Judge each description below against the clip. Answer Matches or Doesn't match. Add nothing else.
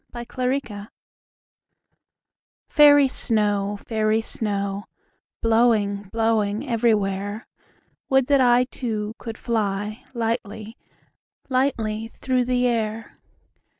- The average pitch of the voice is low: Doesn't match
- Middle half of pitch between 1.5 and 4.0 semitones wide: Matches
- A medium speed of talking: Doesn't match